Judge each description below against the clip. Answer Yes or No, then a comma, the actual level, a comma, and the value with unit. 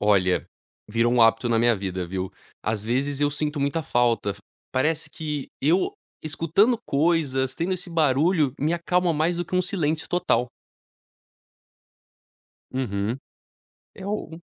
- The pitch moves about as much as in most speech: No, wide, 6.0 semitones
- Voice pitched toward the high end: No, medium, 145 Hz